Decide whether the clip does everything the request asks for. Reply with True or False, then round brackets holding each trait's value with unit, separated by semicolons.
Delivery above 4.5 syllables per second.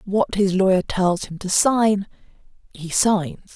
False (3.7 syllables/s)